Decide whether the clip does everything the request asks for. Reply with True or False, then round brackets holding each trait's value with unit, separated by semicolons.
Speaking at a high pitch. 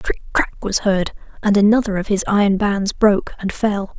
True (200 Hz)